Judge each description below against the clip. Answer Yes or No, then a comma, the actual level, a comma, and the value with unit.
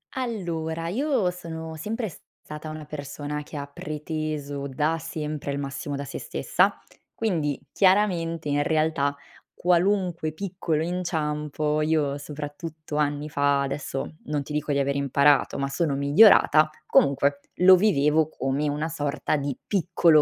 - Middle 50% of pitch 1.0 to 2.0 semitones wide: No, narrow, 2.6 semitones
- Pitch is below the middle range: No, medium, 155 Hz